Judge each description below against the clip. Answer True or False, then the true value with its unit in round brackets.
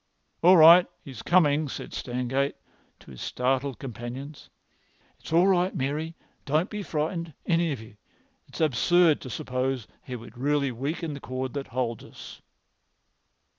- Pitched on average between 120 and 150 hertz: True (140 Hz)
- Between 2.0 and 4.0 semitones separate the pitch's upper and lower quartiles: False (4.4 semitones)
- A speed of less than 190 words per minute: True (145 wpm)